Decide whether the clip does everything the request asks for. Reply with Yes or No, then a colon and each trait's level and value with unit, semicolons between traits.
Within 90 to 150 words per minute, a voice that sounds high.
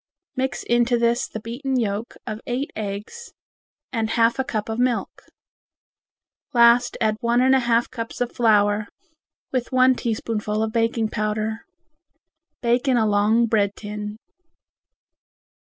Yes: average, 140 wpm; high, 230 Hz